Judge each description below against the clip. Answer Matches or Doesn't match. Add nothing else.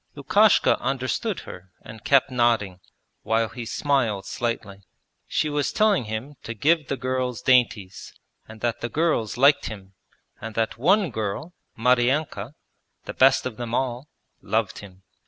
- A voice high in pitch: Doesn't match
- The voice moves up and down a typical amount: Matches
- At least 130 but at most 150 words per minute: Matches